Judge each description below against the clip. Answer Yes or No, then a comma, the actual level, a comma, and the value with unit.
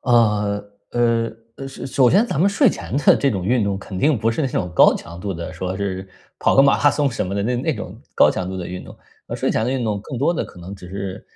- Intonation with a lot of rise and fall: Yes, wide, 5.8 semitones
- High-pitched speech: No, low, 110 Hz